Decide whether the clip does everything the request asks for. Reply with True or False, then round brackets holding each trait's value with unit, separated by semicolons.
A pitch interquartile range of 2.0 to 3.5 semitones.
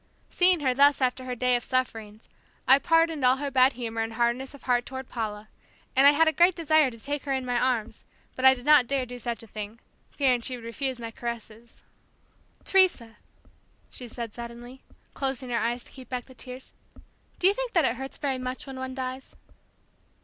True (2.5 semitones)